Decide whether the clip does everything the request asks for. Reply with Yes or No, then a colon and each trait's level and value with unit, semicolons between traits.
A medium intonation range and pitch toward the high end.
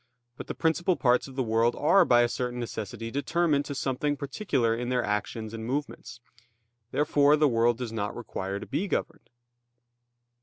No: average, 4.1 semitones; low, 125 Hz